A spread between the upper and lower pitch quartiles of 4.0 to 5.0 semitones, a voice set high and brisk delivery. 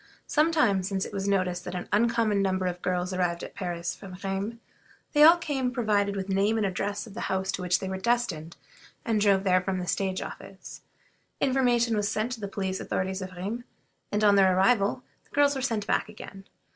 No: average, 3.4 semitones; high, 200 Hz; fast, 215 wpm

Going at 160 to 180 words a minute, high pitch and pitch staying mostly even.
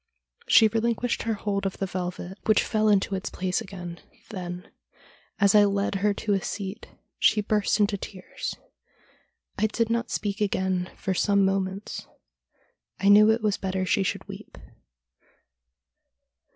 No: average, 150 wpm; high, 200 Hz; narrow, 2.0 semitones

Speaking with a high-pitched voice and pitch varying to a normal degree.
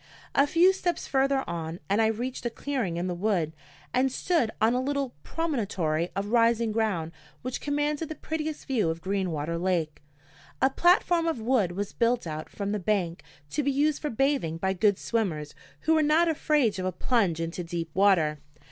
No: high, 220 Hz; wide, 8.0 semitones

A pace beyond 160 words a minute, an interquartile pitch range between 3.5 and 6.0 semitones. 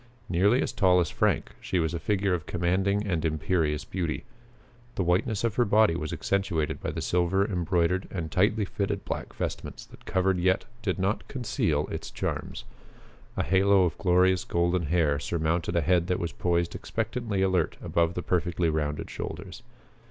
No: average, 170 wpm; narrow, 2.6 semitones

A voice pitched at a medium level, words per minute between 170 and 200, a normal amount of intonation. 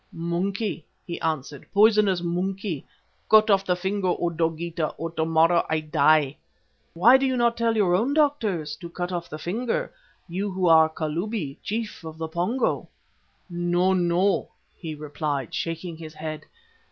No: medium, 175 Hz; average, 155 wpm; average, 3.9 semitones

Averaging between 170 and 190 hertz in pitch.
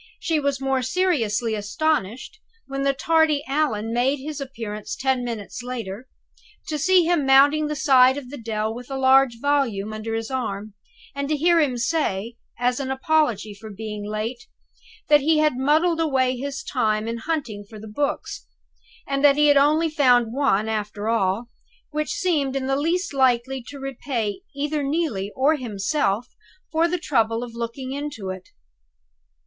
No: very high, 265 Hz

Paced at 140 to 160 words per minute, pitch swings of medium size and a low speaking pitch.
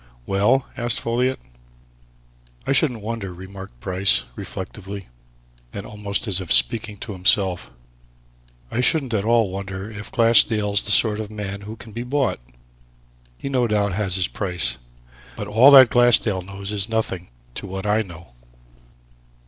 Yes: average, 150 wpm; average, 3.2 semitones; low, 105 Hz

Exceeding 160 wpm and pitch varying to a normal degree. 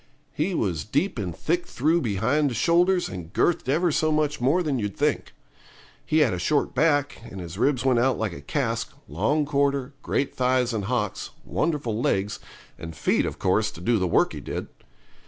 No: average, 190 wpm; wide, 6.6 semitones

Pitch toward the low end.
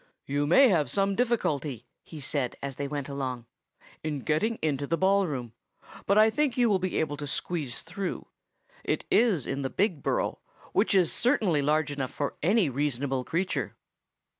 No: medium, 155 Hz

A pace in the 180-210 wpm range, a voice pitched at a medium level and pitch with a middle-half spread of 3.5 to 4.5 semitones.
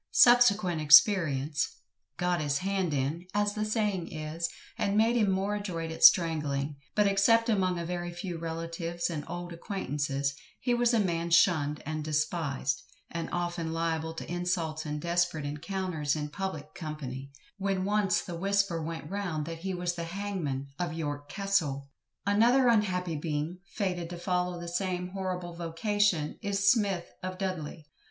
No: average, 155 wpm; medium, 175 Hz; average, 3.9 semitones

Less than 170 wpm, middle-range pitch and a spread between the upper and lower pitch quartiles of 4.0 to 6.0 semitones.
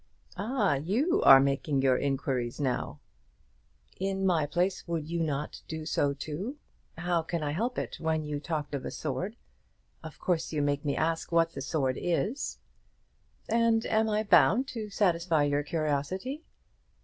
Yes: average, 160 wpm; medium, 160 Hz; average, 5.2 semitones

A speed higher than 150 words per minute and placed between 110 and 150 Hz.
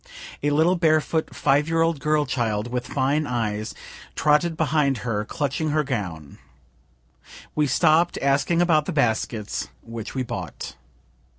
No: slow, 135 wpm; medium, 140 Hz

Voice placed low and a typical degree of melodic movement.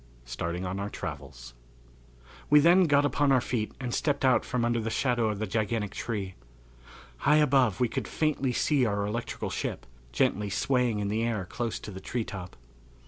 Yes: low, 115 Hz; average, 4.5 semitones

